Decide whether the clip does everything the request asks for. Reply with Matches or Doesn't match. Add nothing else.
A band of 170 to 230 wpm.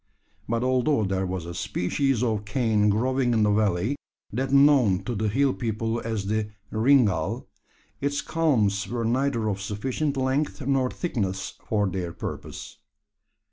Doesn't match